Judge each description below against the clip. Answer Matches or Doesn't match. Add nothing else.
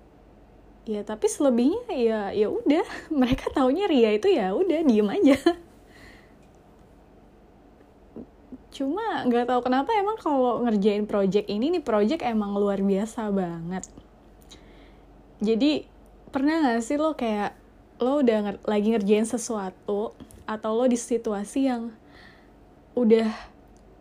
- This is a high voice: Matches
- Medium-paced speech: Matches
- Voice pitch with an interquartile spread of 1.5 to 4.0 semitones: Doesn't match